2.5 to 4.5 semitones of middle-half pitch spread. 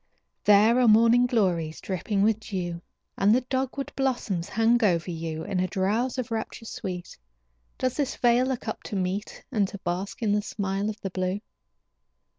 Yes: average, 4.2 semitones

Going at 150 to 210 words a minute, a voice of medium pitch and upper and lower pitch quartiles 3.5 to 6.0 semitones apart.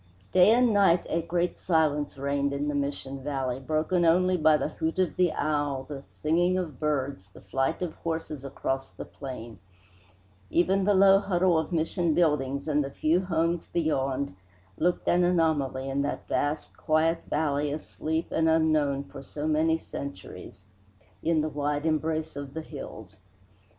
No: average, 160 wpm; medium, 155 Hz; average, 3.1 semitones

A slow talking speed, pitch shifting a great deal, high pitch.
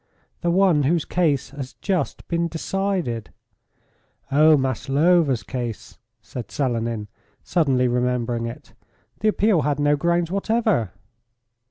No: slow, 115 wpm; wide, 5.7 semitones; medium, 145 Hz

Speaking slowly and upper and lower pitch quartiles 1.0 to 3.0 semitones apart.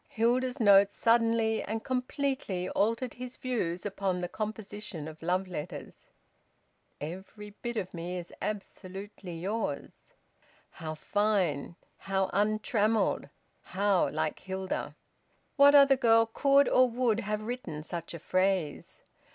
No: slow, 120 wpm; average, 4.1 semitones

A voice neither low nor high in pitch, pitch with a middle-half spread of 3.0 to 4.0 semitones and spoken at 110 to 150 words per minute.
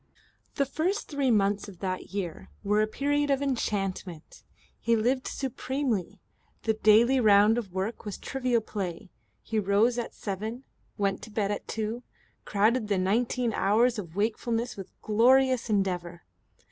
No: high, 215 Hz; average, 3.7 semitones; average, 145 wpm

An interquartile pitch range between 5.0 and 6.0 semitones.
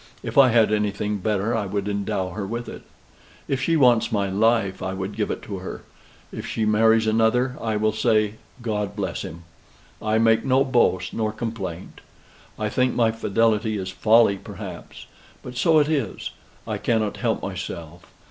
No: narrow, 2.5 semitones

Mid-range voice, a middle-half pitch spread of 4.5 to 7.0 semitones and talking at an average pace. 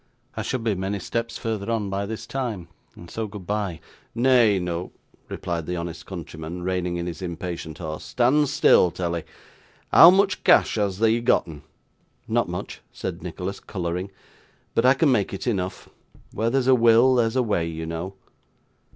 No: low, 100 Hz; average, 5.0 semitones; average, 170 wpm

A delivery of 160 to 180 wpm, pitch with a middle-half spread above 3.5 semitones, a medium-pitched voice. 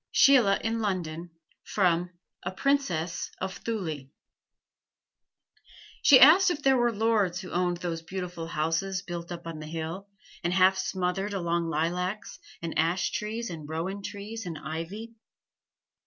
No: average, 140 wpm; average, 3.9 semitones; medium, 180 Hz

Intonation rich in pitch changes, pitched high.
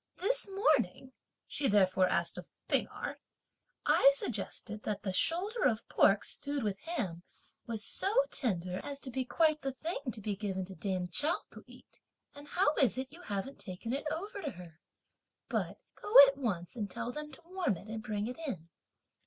Yes: wide, 7.3 semitones; high, 245 Hz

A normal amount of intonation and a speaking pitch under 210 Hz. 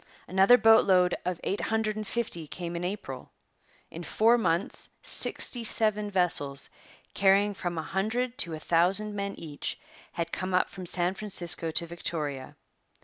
Yes: average, 3.8 semitones; medium, 185 Hz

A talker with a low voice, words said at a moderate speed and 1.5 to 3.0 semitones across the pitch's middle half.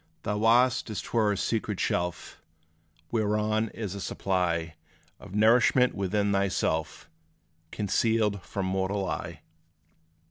No: low, 100 Hz; slow, 115 wpm; narrow, 2.6 semitones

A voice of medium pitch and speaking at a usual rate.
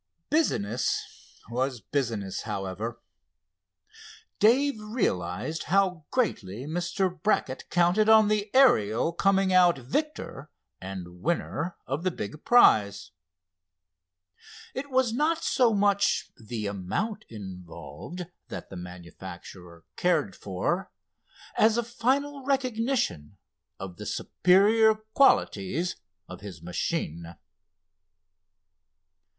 No: medium, 170 Hz; slow, 95 wpm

